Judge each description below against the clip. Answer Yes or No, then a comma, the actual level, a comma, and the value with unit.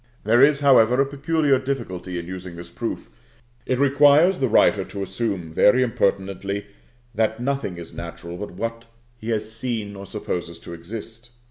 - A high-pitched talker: No, low, 110 Hz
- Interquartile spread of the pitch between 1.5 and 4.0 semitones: No, wide, 5.4 semitones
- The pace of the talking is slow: No, average, 160 wpm